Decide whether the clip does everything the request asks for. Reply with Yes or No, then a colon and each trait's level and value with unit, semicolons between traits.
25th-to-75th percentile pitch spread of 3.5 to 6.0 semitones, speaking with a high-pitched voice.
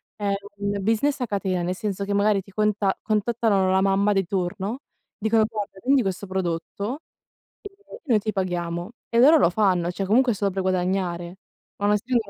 No: average, 2.7 semitones; high, 200 Hz